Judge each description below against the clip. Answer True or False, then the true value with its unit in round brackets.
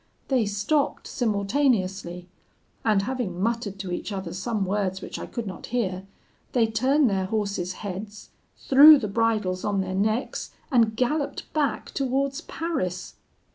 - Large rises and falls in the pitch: False (4.7 semitones)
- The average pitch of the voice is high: True (215 Hz)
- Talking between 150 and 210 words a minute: False (140 wpm)